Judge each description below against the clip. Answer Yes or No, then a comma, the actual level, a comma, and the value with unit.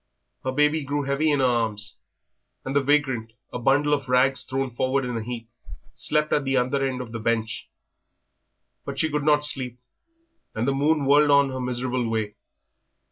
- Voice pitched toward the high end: No, low, 135 Hz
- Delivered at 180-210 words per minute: Yes, average, 185 wpm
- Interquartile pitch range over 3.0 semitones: No, average, 2.7 semitones